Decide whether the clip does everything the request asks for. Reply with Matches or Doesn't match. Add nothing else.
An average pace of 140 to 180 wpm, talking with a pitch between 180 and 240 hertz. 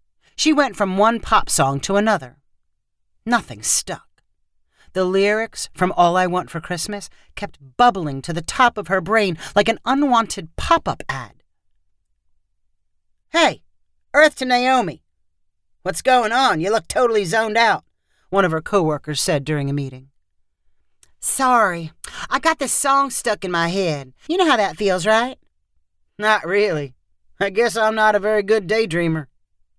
Matches